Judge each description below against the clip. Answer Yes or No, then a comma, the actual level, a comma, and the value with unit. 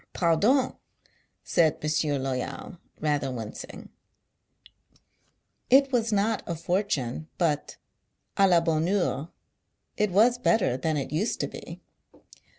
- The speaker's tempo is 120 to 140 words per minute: Yes, slow, 135 wpm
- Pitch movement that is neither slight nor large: No, wide, 5.9 semitones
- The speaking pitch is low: No, medium, 170 Hz